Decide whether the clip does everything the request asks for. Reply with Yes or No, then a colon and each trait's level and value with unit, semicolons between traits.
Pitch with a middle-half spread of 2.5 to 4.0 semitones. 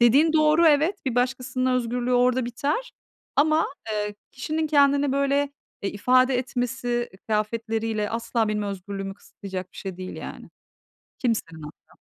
No: average, 4.7 semitones